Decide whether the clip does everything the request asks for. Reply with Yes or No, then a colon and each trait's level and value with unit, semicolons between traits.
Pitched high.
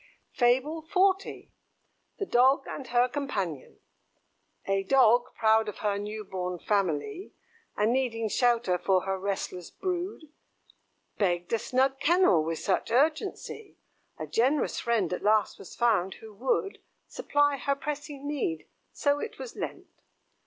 Yes: high, 240 Hz